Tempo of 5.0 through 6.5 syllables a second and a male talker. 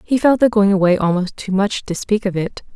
No: 5.5 syllables/s; female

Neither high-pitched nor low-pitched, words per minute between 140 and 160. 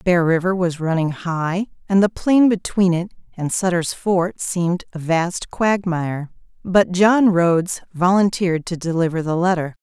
Yes: medium, 180 Hz; average, 155 wpm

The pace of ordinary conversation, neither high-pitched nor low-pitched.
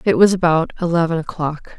Yes: average, 170 wpm; medium, 170 Hz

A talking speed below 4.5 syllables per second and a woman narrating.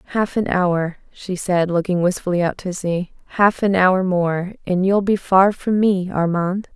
Yes: 4.3 syllables/s; female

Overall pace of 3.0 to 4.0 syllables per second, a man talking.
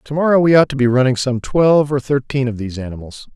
No: 6.5 syllables/s; male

